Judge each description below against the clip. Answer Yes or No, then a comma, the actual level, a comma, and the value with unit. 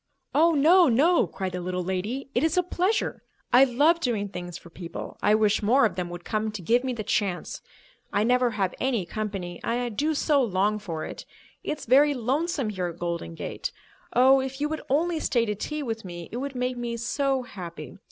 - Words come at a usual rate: No, fast, 210 wpm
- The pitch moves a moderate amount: No, wide, 6.3 semitones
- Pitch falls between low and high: No, high, 235 Hz